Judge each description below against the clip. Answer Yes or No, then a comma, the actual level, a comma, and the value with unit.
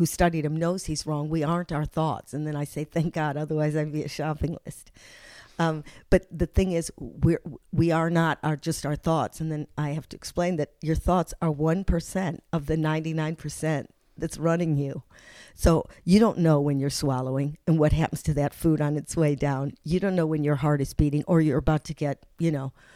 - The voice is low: No, medium, 155 Hz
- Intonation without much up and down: Yes, narrow, 2.0 semitones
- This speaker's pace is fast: Yes, fast, 225 wpm